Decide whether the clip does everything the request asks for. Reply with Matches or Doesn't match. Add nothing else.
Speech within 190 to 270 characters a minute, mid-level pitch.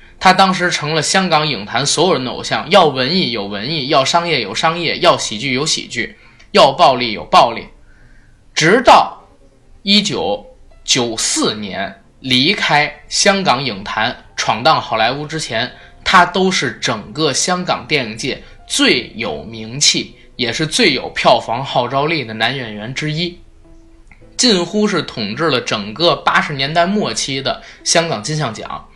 Matches